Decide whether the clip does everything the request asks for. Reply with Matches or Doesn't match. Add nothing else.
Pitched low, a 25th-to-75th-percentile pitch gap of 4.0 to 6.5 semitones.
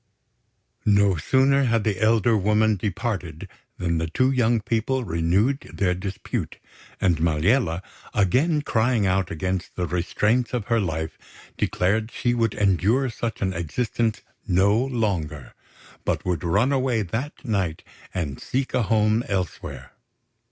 Matches